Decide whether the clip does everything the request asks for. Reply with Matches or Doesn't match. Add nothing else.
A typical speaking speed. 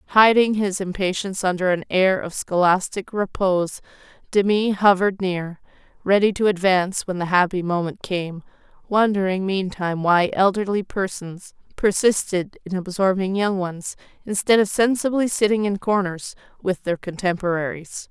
Doesn't match